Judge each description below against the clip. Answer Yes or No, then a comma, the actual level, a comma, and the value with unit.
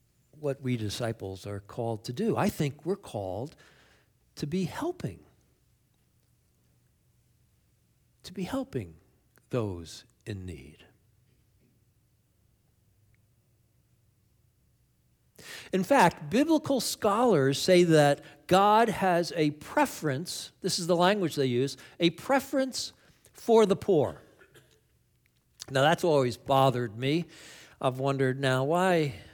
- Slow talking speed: Yes, slow, 100 wpm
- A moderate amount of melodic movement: No, wide, 7.9 semitones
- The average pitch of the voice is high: No, low, 135 Hz